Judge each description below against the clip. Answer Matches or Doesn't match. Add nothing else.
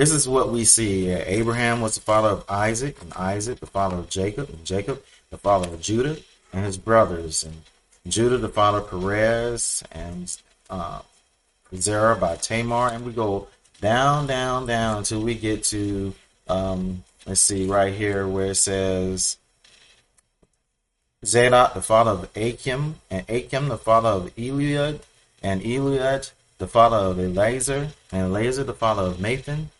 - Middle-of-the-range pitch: Doesn't match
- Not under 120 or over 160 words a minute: Matches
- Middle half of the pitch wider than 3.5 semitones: Matches